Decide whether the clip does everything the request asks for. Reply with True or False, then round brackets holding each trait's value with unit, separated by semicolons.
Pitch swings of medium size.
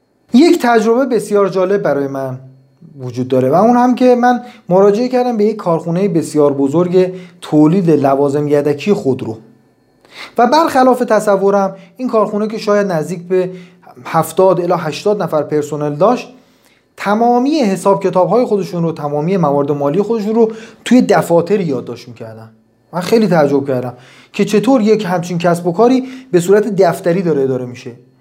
False (6.8 semitones)